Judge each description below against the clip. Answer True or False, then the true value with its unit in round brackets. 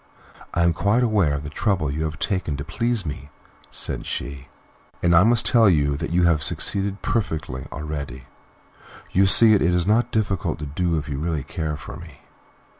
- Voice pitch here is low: True (85 Hz)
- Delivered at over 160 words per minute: True (190 wpm)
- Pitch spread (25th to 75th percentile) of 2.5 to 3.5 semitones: False (5.4 semitones)